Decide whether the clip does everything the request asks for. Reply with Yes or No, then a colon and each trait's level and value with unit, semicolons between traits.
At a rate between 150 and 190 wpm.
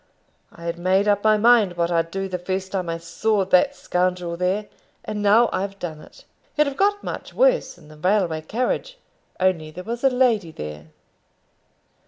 Yes: average, 185 wpm